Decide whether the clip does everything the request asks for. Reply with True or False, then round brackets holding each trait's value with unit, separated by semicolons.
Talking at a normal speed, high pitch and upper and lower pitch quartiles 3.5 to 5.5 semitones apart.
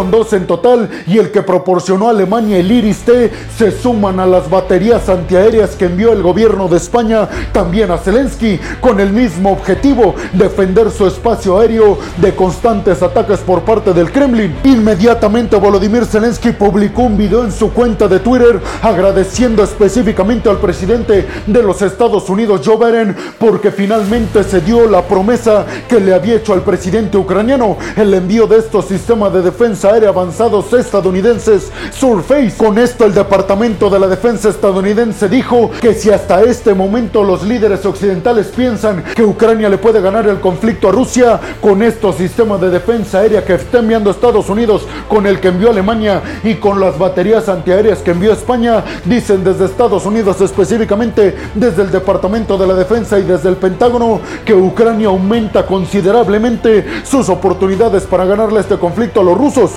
False (165 wpm; 210 Hz; 3.1 semitones)